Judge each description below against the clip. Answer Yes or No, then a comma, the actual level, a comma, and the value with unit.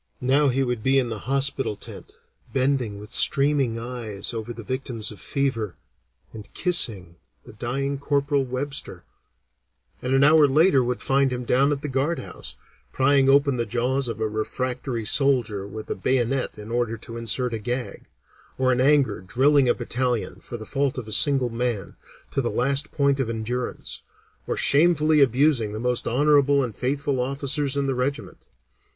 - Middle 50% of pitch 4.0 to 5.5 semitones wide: No, average, 3.1 semitones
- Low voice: Yes, low, 130 Hz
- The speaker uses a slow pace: No, average, 170 wpm